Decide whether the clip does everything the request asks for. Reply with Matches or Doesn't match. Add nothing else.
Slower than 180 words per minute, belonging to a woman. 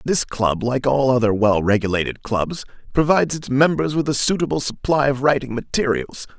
Doesn't match